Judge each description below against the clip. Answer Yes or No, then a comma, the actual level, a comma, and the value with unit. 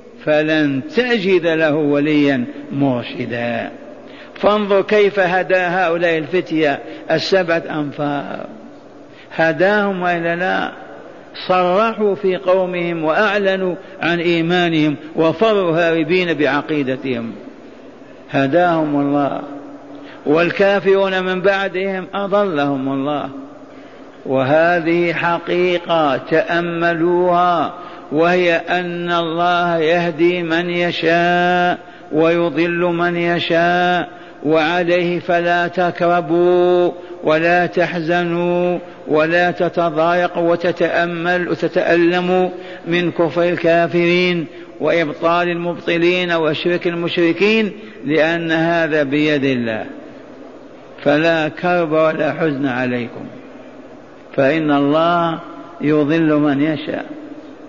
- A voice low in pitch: No, medium, 170 Hz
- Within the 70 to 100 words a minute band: Yes, average, 75 wpm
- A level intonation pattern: Yes, narrow, 1.9 semitones